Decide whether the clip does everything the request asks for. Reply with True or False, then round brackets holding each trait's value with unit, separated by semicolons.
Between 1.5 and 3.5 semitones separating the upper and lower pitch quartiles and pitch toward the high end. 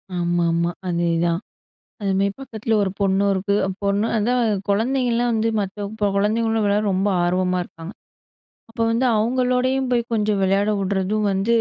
True (3.1 semitones; 205 Hz)